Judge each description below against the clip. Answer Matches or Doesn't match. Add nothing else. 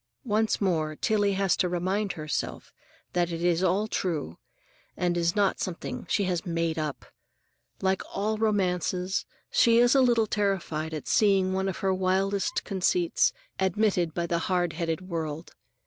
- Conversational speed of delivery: Matches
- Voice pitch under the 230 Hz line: Matches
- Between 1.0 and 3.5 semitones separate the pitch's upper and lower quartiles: Matches